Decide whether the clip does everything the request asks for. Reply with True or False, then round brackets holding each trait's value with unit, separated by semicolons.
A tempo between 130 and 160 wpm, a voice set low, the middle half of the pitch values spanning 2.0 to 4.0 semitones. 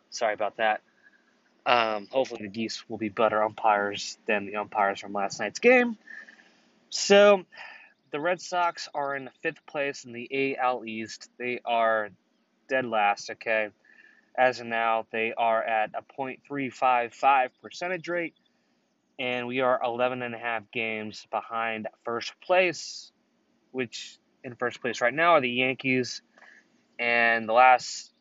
True (140 wpm; 120 Hz; 3.4 semitones)